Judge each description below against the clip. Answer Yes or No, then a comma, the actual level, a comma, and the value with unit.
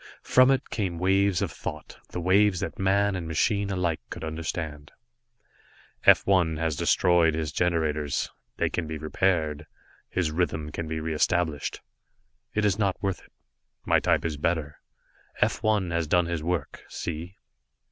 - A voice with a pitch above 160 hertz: No, very low, 85 Hz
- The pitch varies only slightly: No, average, 3.3 semitones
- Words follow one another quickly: No, average, 155 wpm